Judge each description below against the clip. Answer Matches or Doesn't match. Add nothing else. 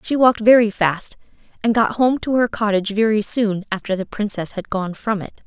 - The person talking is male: Doesn't match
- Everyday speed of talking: Doesn't match